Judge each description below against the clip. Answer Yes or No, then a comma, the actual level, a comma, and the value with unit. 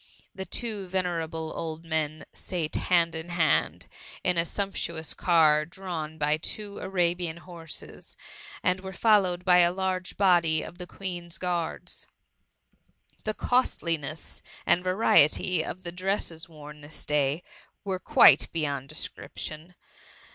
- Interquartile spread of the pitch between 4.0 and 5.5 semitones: No, narrow, 2.6 semitones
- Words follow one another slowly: Yes, slow, 125 wpm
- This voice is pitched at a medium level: Yes, medium, 170 Hz